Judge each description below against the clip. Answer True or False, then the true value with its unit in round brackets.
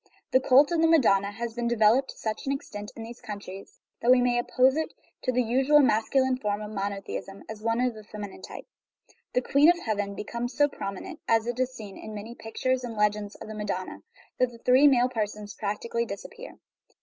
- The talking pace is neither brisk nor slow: False (220 wpm)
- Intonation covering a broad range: False (3.5 semitones)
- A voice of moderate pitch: False (235 Hz)